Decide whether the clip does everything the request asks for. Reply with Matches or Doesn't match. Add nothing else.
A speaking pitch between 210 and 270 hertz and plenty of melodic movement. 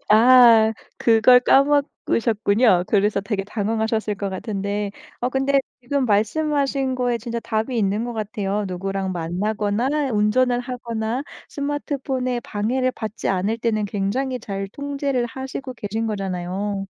Doesn't match